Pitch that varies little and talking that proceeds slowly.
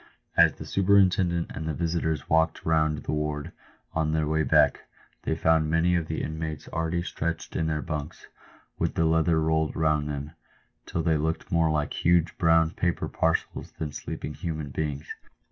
No: narrow, 1.2 semitones; average, 170 wpm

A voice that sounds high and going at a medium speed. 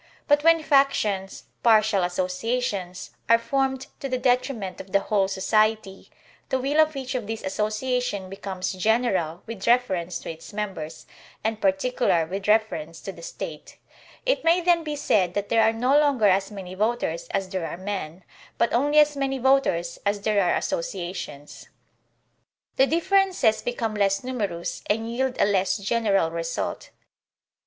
Yes: high, 215 Hz; average, 155 wpm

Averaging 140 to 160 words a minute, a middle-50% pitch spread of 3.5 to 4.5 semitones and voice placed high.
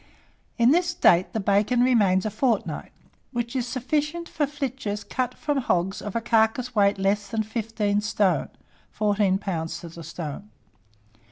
Yes: average, 155 wpm; average, 4.1 semitones; high, 215 Hz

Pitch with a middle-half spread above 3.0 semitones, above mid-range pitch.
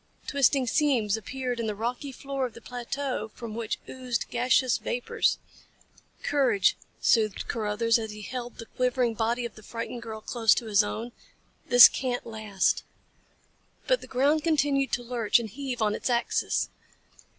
No: average, 2.7 semitones; high, 240 Hz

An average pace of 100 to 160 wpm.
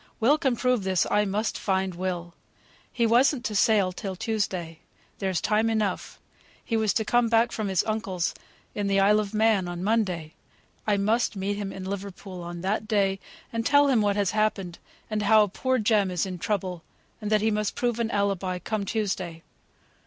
No: average, 190 wpm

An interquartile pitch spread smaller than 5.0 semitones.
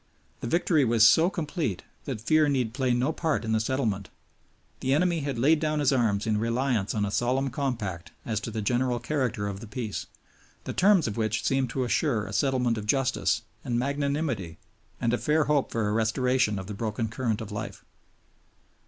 Yes: average, 4.4 semitones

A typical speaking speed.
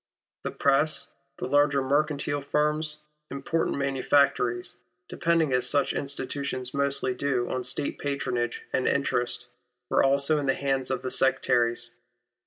No: slow, 130 wpm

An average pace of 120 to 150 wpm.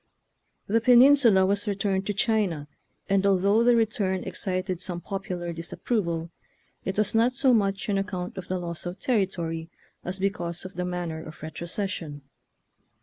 No: average, 165 wpm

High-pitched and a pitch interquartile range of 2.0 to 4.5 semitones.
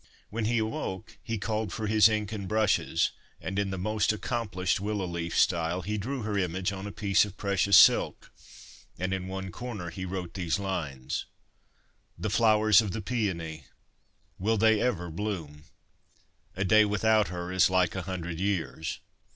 No: low, 100 Hz; average, 3.0 semitones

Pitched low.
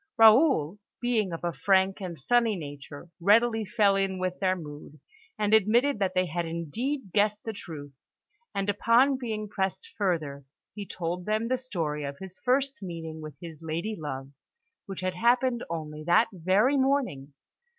No: high, 190 Hz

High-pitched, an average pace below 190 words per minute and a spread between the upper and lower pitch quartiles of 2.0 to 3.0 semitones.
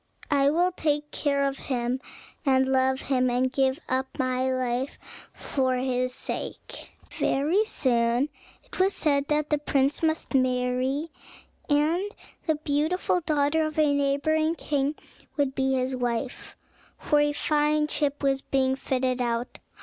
Yes: very high, 275 Hz; average, 145 wpm; narrow, 2.5 semitones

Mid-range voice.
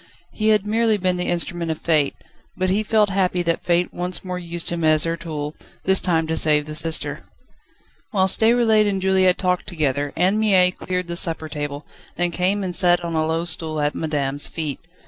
Yes: medium, 175 Hz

